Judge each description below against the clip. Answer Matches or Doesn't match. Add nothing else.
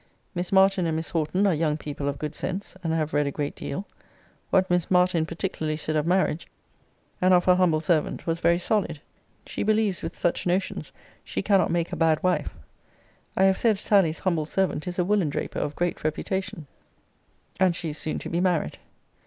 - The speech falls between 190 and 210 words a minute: Matches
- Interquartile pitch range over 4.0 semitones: Doesn't match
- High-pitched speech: Doesn't match